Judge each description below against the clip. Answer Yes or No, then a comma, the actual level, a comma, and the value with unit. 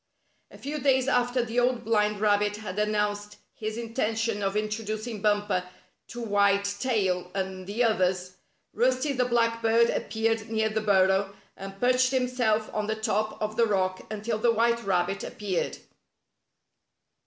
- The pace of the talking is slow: No, average, 150 wpm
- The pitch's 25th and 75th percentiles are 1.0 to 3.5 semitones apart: Yes, narrow, 2.5 semitones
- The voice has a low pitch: No, high, 215 Hz